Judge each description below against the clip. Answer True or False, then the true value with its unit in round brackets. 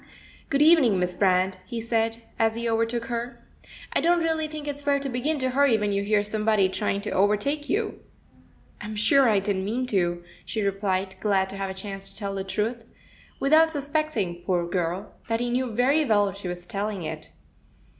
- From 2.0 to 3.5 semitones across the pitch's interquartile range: False (4.9 semitones)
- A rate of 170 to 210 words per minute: True (195 wpm)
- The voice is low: False (215 Hz)